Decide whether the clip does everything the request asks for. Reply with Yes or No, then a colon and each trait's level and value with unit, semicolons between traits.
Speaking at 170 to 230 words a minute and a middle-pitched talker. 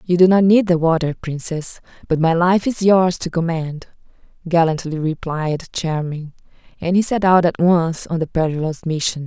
Yes: average, 175 wpm; medium, 170 Hz